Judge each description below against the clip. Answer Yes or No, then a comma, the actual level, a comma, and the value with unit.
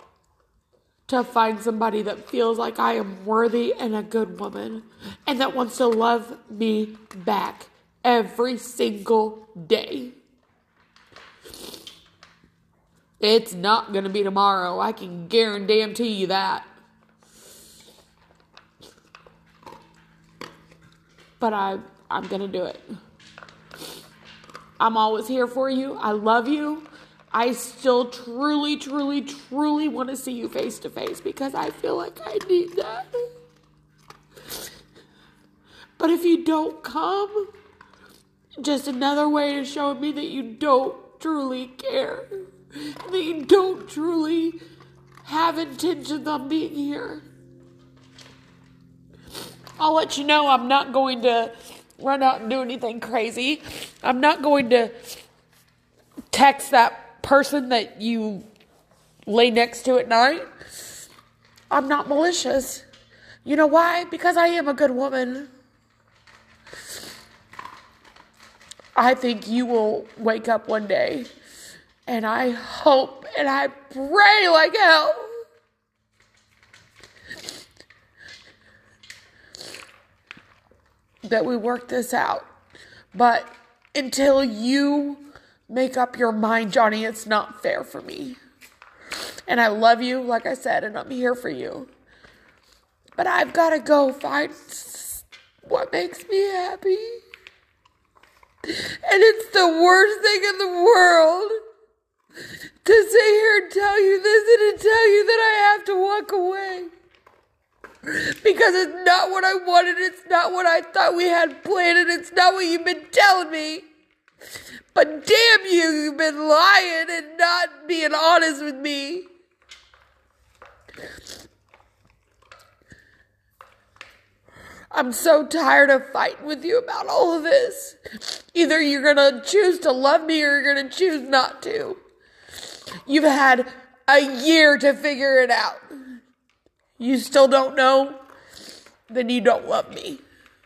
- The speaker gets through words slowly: Yes, slow, 120 wpm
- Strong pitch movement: Yes, wide, 6.3 semitones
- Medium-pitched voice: No, very high, 285 Hz